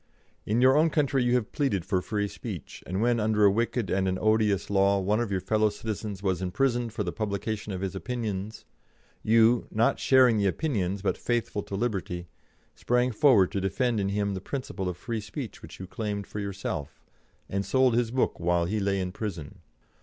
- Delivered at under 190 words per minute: No, average, 200 wpm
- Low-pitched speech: Yes, low, 105 Hz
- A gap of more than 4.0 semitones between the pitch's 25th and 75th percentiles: No, average, 3.4 semitones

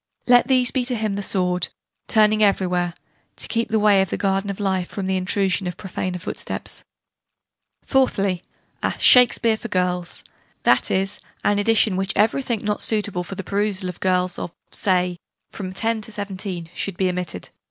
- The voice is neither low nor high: No, high, 195 Hz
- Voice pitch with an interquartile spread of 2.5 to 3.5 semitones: Yes, average, 2.8 semitones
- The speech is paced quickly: No, average, 175 wpm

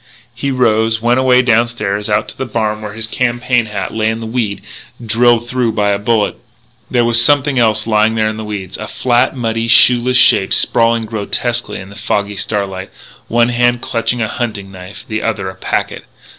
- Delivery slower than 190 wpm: No, average, 195 wpm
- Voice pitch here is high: No, low, 115 Hz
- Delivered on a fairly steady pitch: Yes, narrow, 2.3 semitones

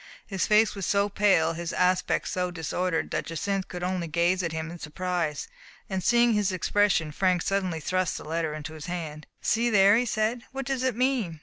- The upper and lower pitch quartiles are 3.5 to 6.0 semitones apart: Yes, average, 3.9 semitones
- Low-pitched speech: No, medium, 185 Hz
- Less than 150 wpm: No, average, 200 wpm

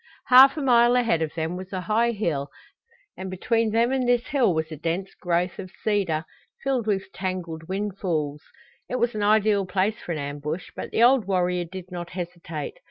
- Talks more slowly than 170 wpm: No, average, 190 wpm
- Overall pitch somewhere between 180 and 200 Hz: Yes, high, 190 Hz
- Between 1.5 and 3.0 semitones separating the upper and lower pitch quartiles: No, average, 5.0 semitones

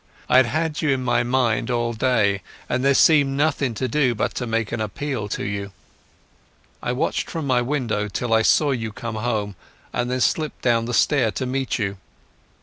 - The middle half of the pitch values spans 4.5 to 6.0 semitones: No, average, 3.4 semitones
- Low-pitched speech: Yes, low, 120 Hz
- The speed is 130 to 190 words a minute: No, average, 200 wpm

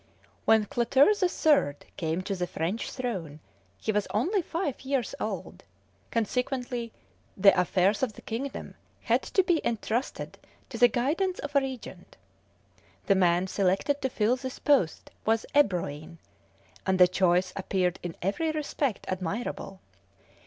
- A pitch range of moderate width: No, wide, 6.5 semitones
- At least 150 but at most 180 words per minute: No, average, 140 wpm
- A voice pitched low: No, high, 220 Hz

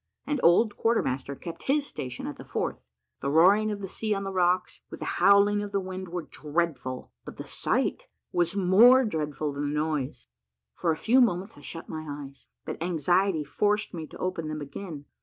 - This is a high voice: No, medium, 175 Hz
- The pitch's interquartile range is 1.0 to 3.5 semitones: No, average, 5.0 semitones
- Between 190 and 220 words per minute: Yes, average, 200 wpm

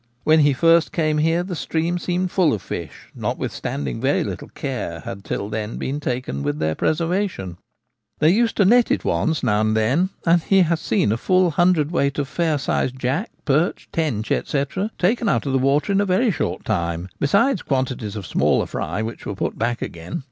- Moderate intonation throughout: No, wide, 8.2 semitones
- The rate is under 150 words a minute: No, average, 195 wpm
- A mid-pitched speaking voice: Yes, medium, 150 Hz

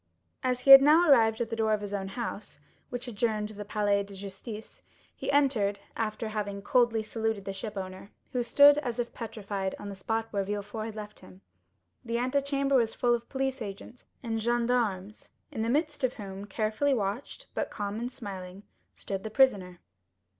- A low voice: No, high, 220 Hz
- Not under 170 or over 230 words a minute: Yes, average, 185 wpm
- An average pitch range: Yes, average, 3.3 semitones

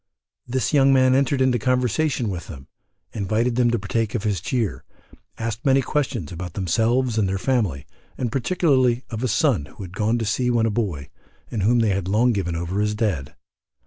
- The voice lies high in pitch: No, low, 115 Hz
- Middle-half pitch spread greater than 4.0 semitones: Yes, average, 4.4 semitones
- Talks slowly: No, average, 195 wpm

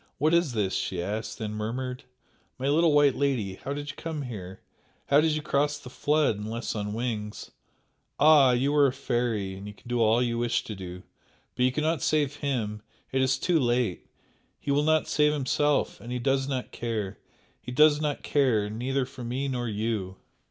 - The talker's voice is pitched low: Yes, low, 125 Hz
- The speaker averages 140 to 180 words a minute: No, average, 195 wpm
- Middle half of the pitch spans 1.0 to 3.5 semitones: No, average, 4.9 semitones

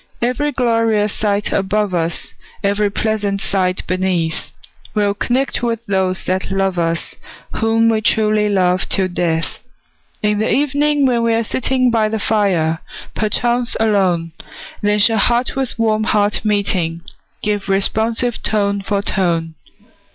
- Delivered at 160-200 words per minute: No, slow, 135 wpm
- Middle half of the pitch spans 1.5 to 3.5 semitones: Yes, average, 3.1 semitones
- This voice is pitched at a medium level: No, high, 210 Hz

